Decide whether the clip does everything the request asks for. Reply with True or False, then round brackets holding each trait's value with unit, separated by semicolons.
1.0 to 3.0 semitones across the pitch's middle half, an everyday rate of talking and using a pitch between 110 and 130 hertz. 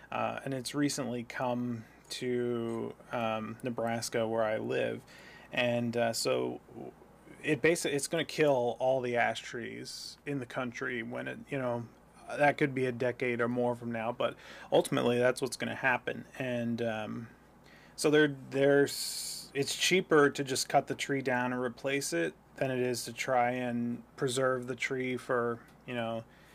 True (2.6 semitones; 165 wpm; 125 Hz)